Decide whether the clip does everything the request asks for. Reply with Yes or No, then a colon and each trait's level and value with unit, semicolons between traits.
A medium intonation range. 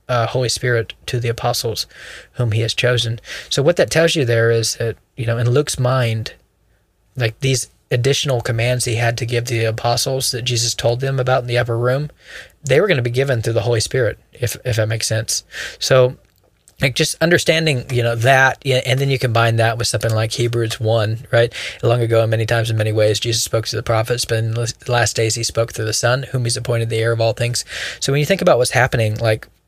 No: narrow, 2.0 semitones